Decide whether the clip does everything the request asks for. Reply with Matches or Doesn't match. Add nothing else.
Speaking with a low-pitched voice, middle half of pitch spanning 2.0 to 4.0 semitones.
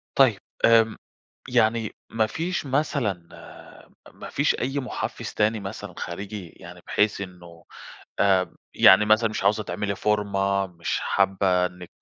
Matches